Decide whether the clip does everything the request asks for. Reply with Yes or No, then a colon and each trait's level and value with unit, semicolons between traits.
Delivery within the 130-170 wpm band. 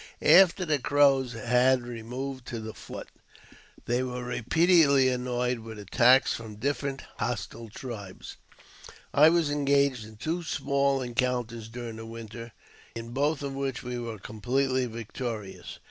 Yes: slow, 135 wpm